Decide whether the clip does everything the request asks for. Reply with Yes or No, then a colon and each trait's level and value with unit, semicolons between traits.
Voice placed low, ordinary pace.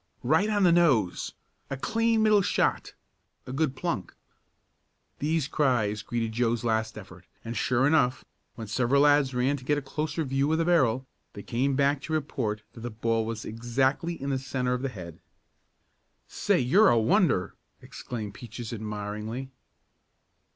Yes: low, 130 Hz; average, 160 wpm